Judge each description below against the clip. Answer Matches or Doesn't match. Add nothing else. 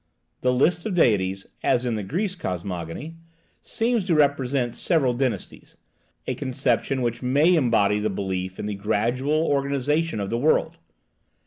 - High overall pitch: Doesn't match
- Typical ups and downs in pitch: Doesn't match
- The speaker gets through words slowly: Doesn't match